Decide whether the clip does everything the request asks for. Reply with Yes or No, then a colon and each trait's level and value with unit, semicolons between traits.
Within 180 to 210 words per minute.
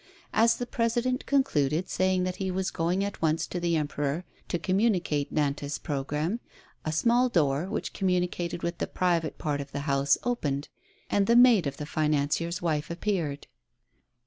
No: average, 165 wpm